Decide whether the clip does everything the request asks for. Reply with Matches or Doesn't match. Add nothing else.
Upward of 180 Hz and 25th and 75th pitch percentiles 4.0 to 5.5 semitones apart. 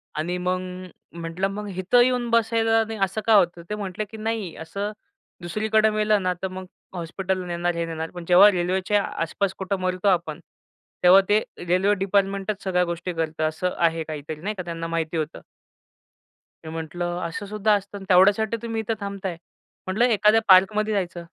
Doesn't match